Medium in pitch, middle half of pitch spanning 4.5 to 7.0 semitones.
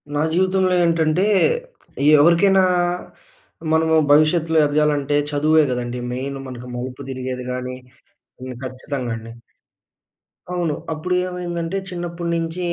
Yes: medium, 155 Hz; average, 4.9 semitones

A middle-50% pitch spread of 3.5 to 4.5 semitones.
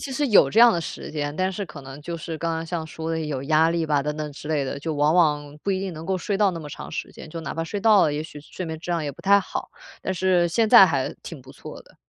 Yes: average, 3.8 semitones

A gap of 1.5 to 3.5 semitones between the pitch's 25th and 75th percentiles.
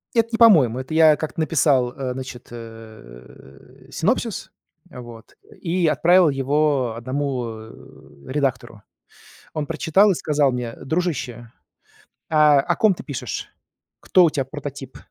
No: average, 4.5 semitones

